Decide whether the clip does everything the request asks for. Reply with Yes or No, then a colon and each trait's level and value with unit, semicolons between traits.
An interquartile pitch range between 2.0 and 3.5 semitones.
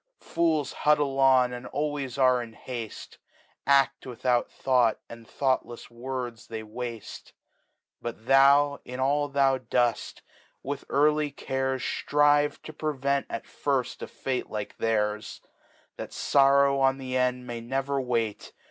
Yes: narrow, 2.5 semitones